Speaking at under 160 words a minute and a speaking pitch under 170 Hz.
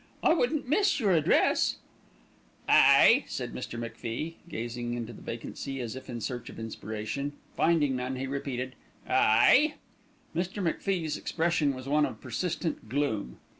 Yes: slow, 135 wpm; low, 135 Hz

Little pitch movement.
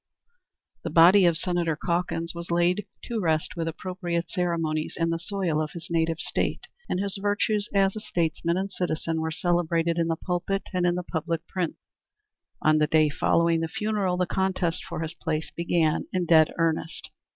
Yes: narrow, 1.9 semitones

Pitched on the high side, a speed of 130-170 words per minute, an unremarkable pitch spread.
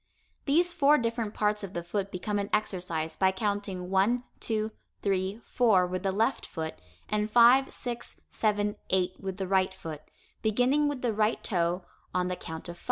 No: high, 205 Hz; average, 180 wpm; average, 3.7 semitones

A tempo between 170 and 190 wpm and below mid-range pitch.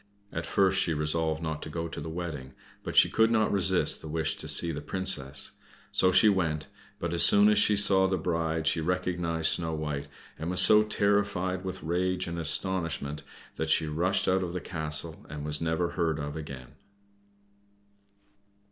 Yes: average, 185 wpm; very low, 85 Hz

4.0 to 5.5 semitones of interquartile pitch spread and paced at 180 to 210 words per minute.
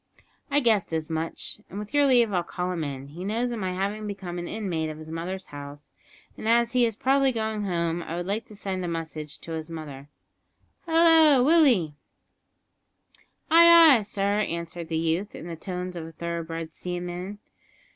Yes: average, 5.1 semitones; average, 185 wpm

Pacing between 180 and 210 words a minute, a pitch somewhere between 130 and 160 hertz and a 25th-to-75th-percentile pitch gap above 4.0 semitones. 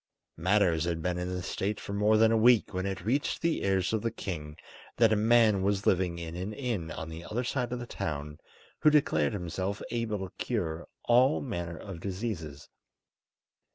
No: average, 190 wpm; low, 100 Hz; average, 4.8 semitones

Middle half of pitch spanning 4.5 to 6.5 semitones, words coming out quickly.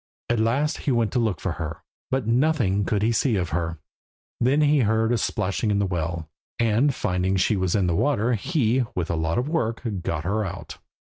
Yes: average, 5.1 semitones; fast, 210 wpm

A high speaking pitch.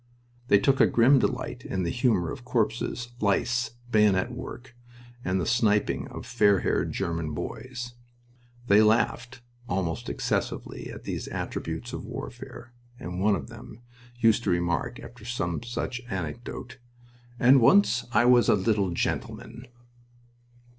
No: low, 115 Hz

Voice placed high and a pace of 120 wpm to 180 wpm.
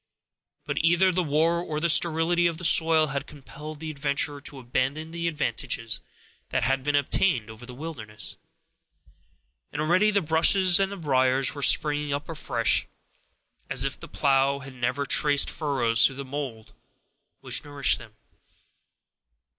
No: medium, 145 Hz; average, 150 wpm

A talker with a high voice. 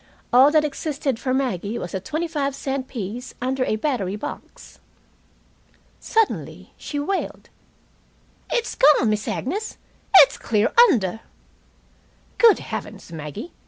Yes: very high, 265 Hz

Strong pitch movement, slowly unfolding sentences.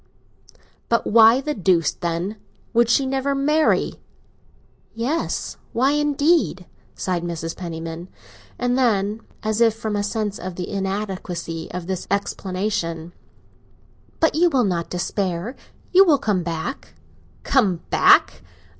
Yes: wide, 6.3 semitones; slow, 120 wpm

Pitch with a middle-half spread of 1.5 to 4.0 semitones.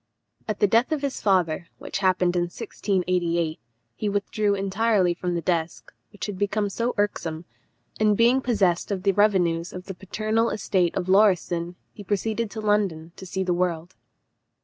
Yes: average, 3.1 semitones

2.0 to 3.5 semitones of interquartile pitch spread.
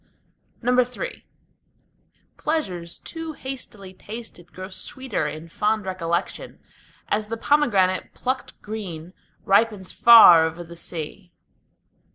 No: wide, 5.5 semitones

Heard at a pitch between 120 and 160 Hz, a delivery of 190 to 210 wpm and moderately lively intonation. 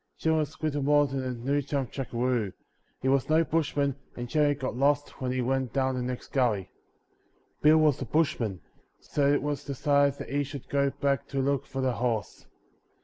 No: medium, 140 Hz; average, 195 wpm; narrow, 2.2 semitones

